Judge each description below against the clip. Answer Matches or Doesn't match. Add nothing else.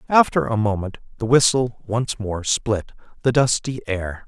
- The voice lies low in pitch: Matches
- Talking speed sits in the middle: Matches